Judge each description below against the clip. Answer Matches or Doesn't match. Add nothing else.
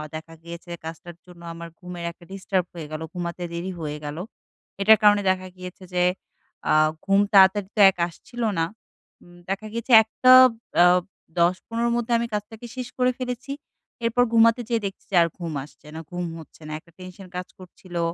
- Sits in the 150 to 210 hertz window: Matches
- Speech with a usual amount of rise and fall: Matches